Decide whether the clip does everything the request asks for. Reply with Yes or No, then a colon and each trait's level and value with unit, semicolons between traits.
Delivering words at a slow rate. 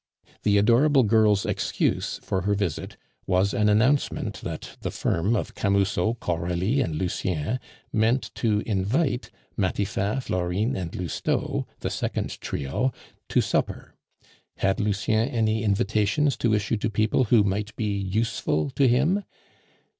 Yes: slow, 130 wpm